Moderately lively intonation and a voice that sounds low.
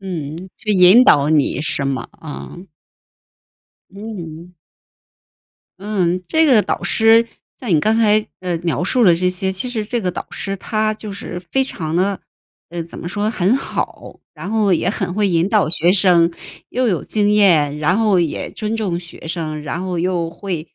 No: average, 4.1 semitones; medium, 185 Hz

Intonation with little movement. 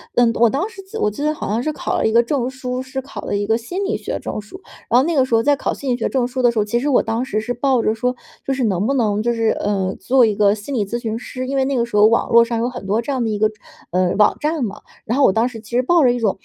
No: average, 3.4 semitones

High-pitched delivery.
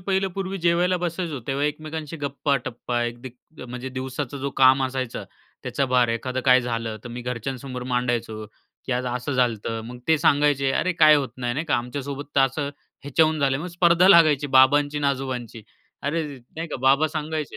No: low, 135 Hz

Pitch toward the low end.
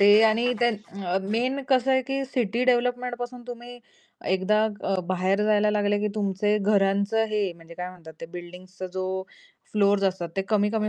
No: high, 210 Hz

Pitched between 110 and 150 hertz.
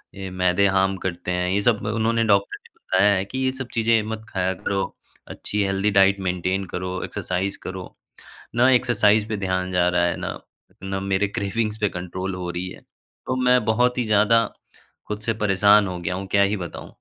No: low, 100 Hz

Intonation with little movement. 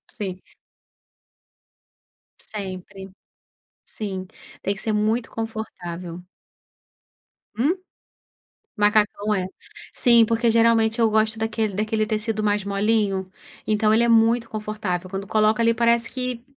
Yes: narrow, 2.2 semitones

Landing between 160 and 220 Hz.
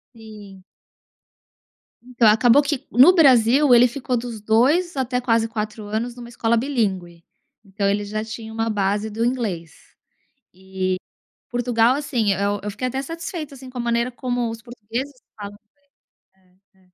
No: high, 230 Hz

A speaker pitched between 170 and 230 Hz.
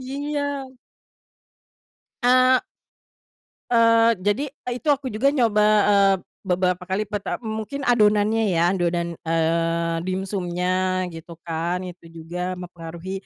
Yes: high, 190 Hz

